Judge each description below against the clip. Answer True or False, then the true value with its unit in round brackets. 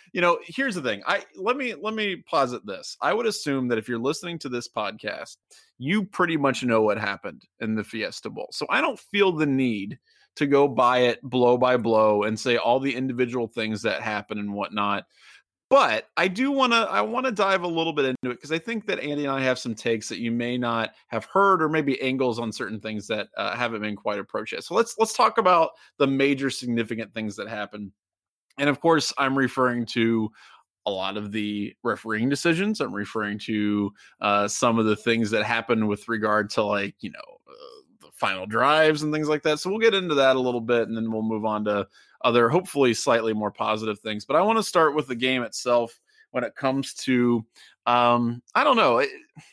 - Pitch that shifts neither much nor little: False (5.8 semitones)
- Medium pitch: False (125 Hz)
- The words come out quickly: True (220 wpm)